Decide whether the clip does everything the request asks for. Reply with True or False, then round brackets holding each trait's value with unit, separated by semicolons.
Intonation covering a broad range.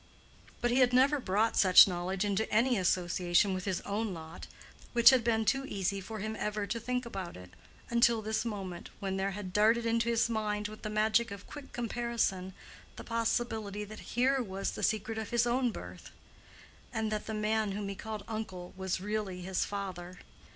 False (3.2 semitones)